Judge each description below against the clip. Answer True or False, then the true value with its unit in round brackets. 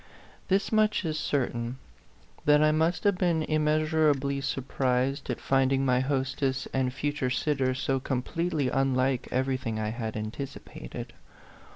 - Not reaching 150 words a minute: True (135 wpm)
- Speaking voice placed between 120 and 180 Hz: True (135 Hz)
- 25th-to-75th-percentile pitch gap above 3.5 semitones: False (3.0 semitones)